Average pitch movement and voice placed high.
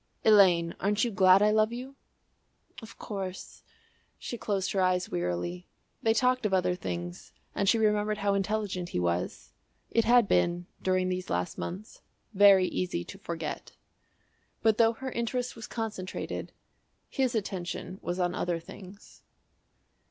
Yes: average, 3.4 semitones; high, 195 Hz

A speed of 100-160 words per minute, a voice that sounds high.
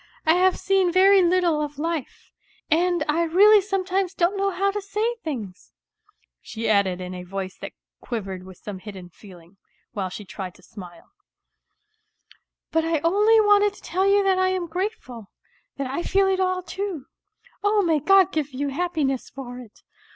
No: average, 175 wpm; very high, 335 Hz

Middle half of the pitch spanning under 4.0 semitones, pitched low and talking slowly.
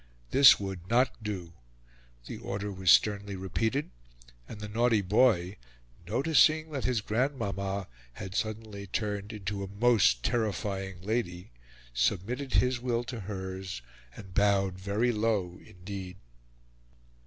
Yes: average, 3.5 semitones; low, 100 Hz; slow, 120 wpm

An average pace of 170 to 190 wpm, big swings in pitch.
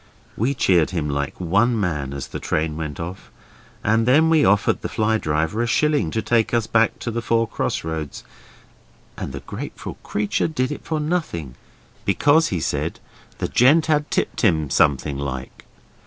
Yes: average, 175 wpm; wide, 8.1 semitones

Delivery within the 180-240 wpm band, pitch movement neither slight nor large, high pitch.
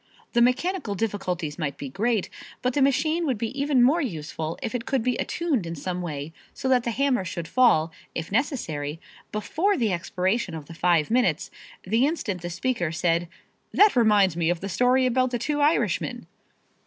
No: average, 185 wpm; wide, 7.1 semitones; high, 220 Hz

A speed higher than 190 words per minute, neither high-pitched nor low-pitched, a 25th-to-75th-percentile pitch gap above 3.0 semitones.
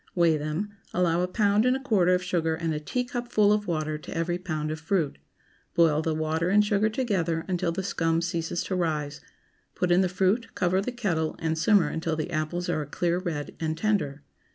Yes: fast, 205 wpm; medium, 175 Hz; average, 3.8 semitones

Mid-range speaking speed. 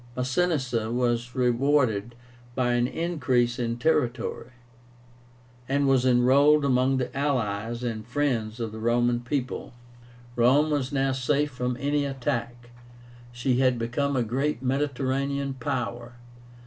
No: slow, 120 wpm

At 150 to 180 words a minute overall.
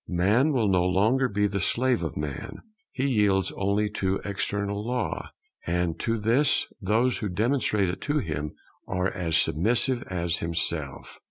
Yes: average, 155 wpm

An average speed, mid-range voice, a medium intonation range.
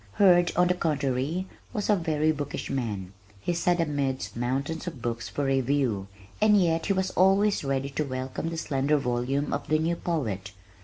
Yes: average, 175 wpm; medium, 145 Hz; average, 4.8 semitones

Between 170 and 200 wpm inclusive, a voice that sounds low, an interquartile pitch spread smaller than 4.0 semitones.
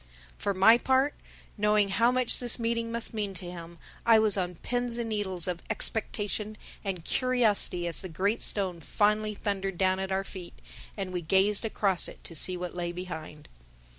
No: average, 180 wpm; high, 200 Hz; average, 3.6 semitones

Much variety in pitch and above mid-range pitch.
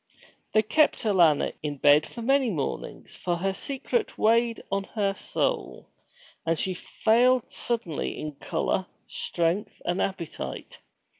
Yes: wide, 5.9 semitones; high, 195 Hz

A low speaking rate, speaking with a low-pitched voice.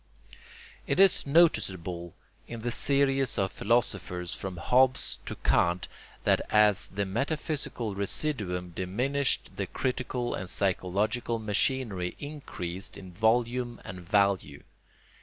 Yes: slow, 110 wpm; low, 105 Hz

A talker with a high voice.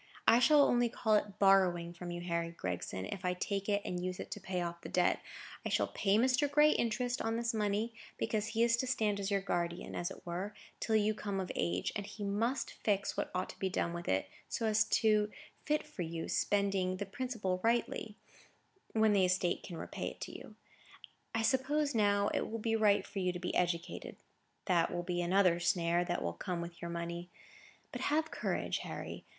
Yes: high, 200 Hz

